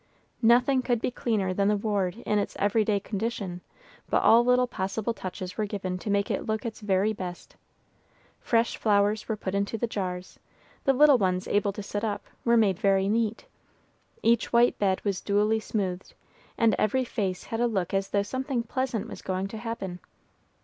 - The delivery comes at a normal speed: Yes, average, 185 wpm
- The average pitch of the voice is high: Yes, high, 210 Hz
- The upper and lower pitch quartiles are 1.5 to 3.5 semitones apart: Yes, average, 3.0 semitones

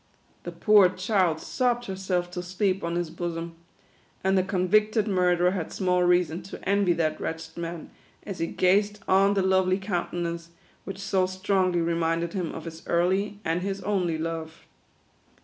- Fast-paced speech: No, average, 165 wpm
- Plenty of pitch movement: No, narrow, 2.4 semitones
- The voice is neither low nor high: Yes, medium, 180 Hz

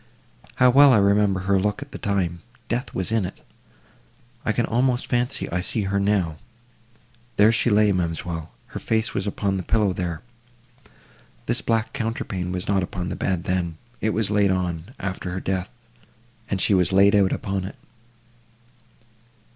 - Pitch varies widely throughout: No, average, 3.6 semitones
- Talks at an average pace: Yes, average, 155 wpm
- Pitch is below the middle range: Yes, low, 100 Hz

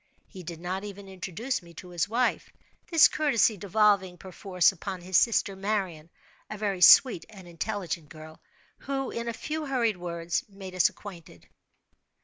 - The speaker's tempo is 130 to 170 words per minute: Yes, average, 150 wpm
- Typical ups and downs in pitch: Yes, average, 3.7 semitones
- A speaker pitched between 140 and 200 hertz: Yes, high, 190 Hz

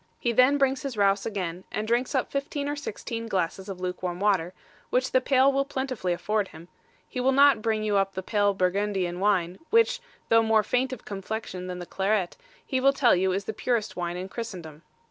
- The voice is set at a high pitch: Yes, high, 210 Hz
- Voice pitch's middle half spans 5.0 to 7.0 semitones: Yes, wide, 5.4 semitones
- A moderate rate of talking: No, fast, 210 wpm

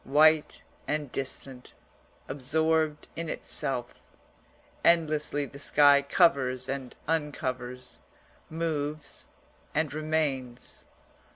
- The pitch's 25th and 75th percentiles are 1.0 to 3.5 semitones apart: Yes, average, 3.0 semitones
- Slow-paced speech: Yes, slow, 80 wpm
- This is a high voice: No, medium, 145 Hz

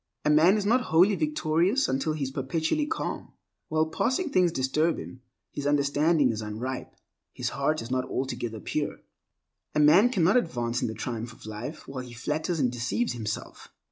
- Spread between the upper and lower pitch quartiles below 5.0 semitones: No, average, 5.3 semitones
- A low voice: No, medium, 150 Hz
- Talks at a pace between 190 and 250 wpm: No, average, 175 wpm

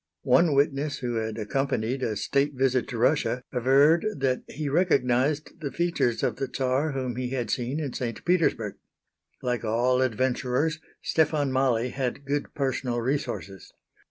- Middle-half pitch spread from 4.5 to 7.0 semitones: No, average, 2.7 semitones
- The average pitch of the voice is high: No, low, 130 Hz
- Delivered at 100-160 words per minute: Yes, average, 150 wpm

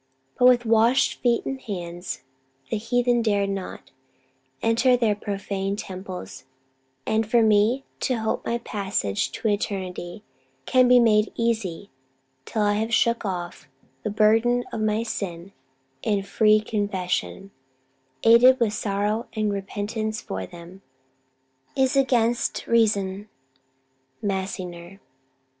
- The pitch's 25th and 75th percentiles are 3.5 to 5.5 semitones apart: No, average, 2.9 semitones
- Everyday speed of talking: No, slow, 120 wpm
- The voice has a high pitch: Yes, high, 215 Hz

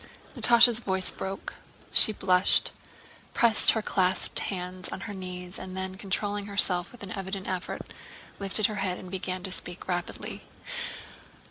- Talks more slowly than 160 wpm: Yes, average, 145 wpm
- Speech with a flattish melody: Yes, narrow, 1.9 semitones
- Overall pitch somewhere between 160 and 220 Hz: Yes, high, 190 Hz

